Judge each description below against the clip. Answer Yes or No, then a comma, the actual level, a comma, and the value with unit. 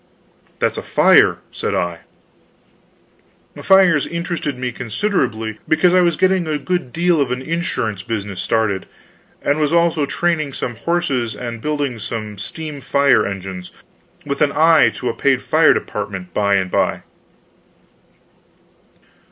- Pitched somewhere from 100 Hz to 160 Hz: Yes, medium, 140 Hz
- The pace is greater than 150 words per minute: No, slow, 135 wpm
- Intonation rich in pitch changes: Yes, wide, 7.3 semitones